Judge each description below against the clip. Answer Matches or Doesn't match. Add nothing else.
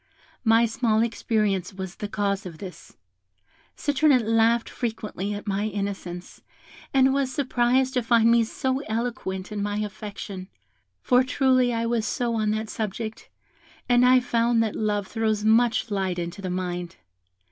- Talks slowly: Doesn't match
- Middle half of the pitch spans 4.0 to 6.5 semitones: Doesn't match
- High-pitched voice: Matches